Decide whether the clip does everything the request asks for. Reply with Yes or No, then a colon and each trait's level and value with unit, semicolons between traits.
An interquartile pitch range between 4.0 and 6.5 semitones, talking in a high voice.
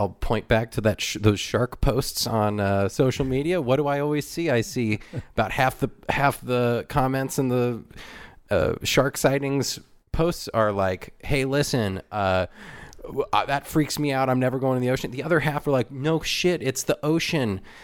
No: average, 4.4 semitones; low, 130 Hz